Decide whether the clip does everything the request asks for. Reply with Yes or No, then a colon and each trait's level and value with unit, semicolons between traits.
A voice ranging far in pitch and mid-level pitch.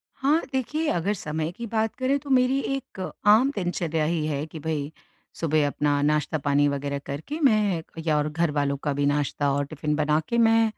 Yes: wide, 7.5 semitones; medium, 160 Hz